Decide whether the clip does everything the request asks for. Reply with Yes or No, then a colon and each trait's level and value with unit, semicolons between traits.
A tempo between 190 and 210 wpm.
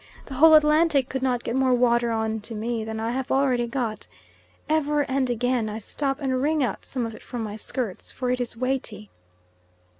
Yes: fast, 205 wpm